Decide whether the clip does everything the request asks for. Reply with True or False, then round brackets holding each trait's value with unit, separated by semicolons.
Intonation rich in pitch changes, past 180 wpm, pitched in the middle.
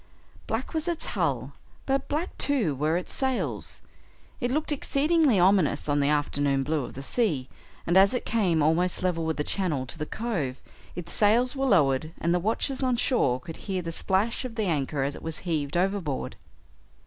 True (8.0 semitones; 190 wpm; 180 Hz)